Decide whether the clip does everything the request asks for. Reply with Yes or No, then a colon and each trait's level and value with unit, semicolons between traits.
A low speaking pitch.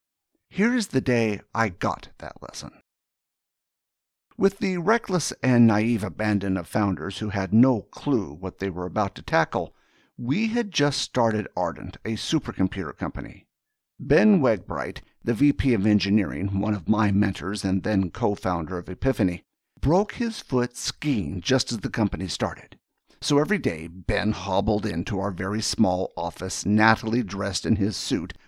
Yes: low, 105 Hz